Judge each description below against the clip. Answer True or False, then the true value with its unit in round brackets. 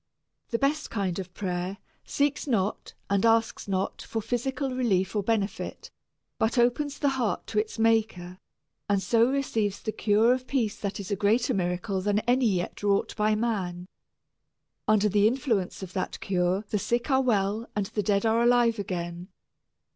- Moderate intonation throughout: True (3.6 semitones)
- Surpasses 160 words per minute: True (170 wpm)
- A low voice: False (215 Hz)